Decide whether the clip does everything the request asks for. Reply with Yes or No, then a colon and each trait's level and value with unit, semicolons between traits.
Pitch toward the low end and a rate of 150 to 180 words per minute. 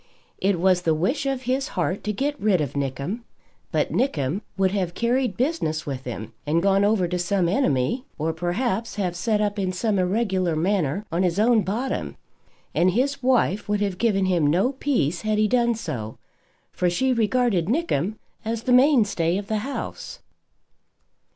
No: high, 200 Hz; average, 175 wpm